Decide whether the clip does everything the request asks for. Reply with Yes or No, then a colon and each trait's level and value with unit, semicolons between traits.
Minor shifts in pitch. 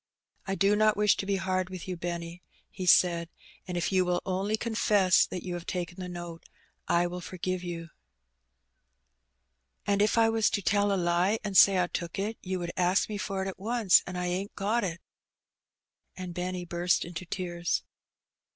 Yes: narrow, 2.2 semitones